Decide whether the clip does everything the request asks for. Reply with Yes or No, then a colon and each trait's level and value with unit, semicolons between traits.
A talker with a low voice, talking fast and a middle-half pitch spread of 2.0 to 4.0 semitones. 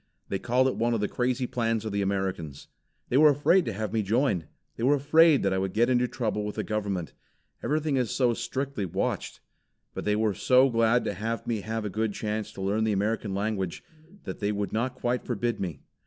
Yes: low, 110 Hz; fast, 220 wpm; average, 3.5 semitones